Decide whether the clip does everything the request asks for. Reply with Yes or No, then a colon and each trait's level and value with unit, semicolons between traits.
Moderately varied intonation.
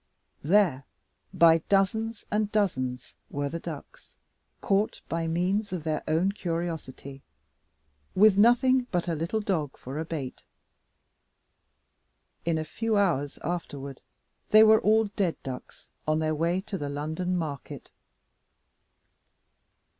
Yes: average, 5.0 semitones